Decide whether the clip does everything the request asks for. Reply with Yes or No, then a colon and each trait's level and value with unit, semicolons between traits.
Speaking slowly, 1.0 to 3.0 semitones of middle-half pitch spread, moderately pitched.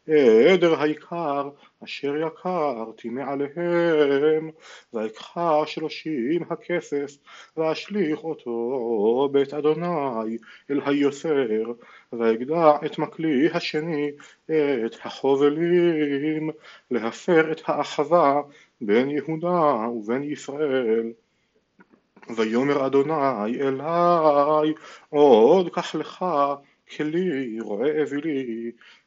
Yes: slow, 75 wpm; average, 2.7 semitones; medium, 150 Hz